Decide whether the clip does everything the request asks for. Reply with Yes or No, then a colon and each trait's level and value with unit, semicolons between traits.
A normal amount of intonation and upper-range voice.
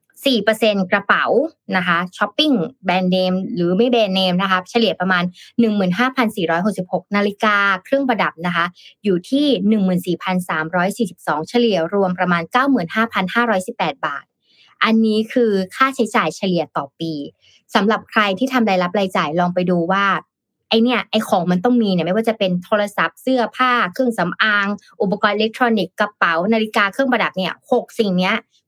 Yes: average, 4.3 semitones; high, 205 Hz